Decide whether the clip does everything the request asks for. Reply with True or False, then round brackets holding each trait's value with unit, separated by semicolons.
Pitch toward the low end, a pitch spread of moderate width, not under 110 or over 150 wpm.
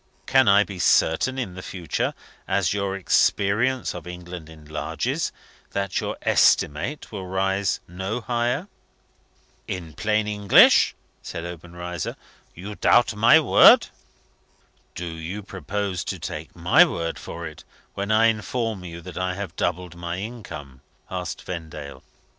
True (95 Hz; 3.4 semitones; 135 wpm)